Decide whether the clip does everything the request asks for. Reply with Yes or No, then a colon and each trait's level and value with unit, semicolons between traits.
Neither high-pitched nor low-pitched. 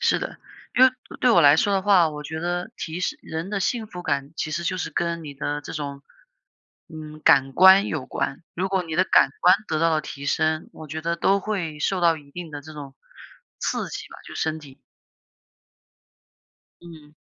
Yes: medium, 160 Hz